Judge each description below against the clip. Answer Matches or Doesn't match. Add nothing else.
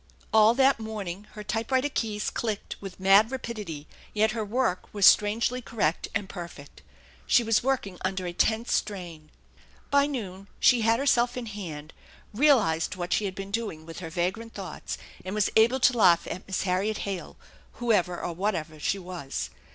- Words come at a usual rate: Matches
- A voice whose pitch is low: Doesn't match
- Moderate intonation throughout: Matches